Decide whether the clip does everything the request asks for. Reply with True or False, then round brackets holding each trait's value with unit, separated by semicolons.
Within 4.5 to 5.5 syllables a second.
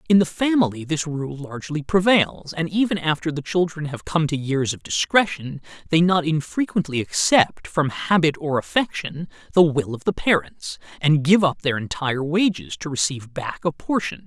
True (5.0 syllables/s)